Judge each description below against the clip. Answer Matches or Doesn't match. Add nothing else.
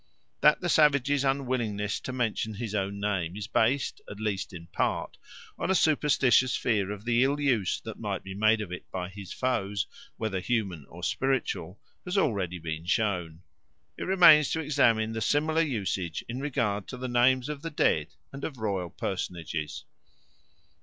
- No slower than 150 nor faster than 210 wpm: Matches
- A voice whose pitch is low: Matches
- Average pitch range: Doesn't match